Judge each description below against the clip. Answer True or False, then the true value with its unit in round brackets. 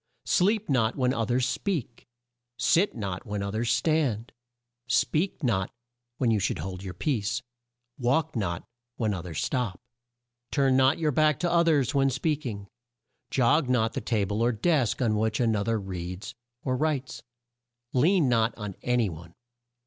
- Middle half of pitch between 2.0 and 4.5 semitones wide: False (5.1 semitones)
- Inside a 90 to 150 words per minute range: False (170 wpm)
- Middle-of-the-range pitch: False (120 Hz)